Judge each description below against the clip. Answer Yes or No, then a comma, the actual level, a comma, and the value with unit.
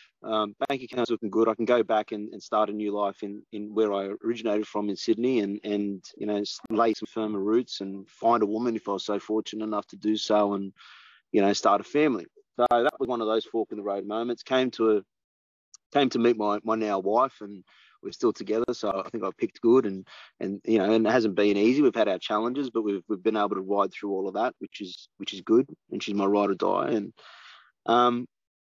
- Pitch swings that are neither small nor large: No, narrow, 2.0 semitones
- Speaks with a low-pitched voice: Yes, low, 105 Hz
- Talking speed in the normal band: No, fast, 245 wpm